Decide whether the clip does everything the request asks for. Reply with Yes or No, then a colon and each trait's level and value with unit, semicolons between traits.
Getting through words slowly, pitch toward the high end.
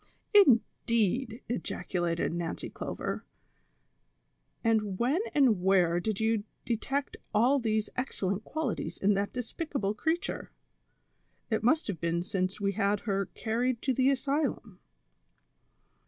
Yes: slow, 125 wpm; high, 220 Hz